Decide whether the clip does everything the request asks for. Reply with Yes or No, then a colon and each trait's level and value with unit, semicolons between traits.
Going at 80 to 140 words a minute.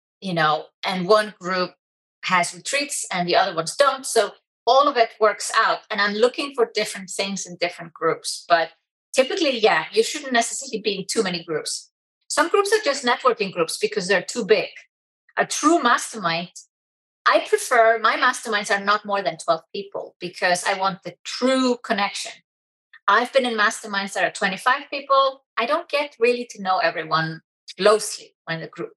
No: average, 180 wpm